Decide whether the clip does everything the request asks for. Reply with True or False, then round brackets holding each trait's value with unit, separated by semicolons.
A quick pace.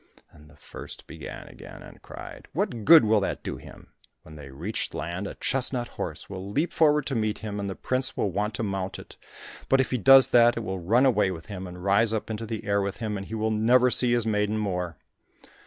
True (235 wpm)